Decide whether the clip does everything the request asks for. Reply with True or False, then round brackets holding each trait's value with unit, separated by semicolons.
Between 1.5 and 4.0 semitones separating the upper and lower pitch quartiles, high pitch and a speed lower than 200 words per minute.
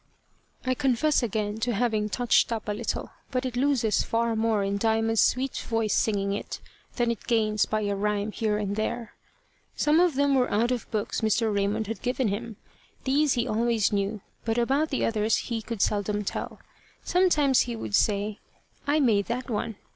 True (2.9 semitones; 225 Hz; 185 wpm)